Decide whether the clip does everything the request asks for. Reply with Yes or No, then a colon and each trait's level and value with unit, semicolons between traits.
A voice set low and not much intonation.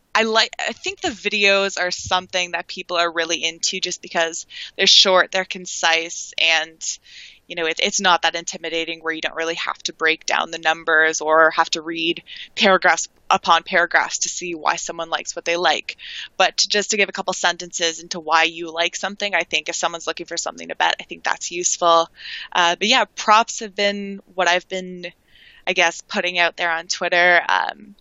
No: medium, 175 Hz; narrow, 2.3 semitones